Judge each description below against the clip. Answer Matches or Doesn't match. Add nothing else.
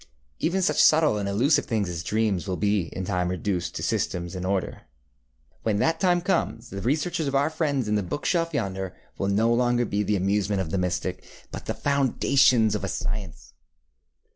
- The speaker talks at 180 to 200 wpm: Matches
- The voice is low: Matches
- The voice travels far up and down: Matches